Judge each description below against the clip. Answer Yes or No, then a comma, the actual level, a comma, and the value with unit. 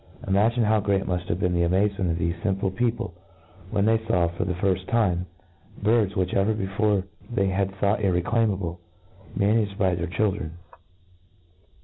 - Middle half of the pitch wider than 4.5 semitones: No, average, 2.8 semitones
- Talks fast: No, average, 155 wpm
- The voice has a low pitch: Yes, very low, 95 Hz